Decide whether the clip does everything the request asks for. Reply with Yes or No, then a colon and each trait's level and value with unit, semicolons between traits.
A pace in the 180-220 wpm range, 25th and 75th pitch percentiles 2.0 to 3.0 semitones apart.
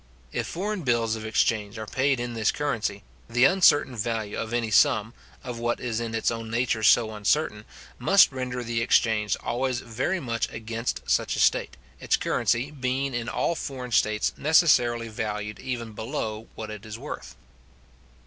No: average, 170 wpm; average, 2.7 semitones